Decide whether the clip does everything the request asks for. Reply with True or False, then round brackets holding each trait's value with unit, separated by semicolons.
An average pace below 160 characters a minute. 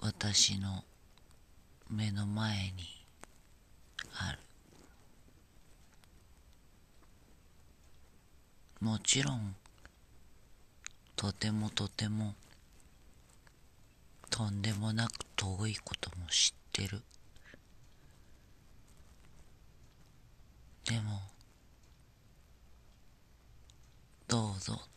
True (90 characters per minute)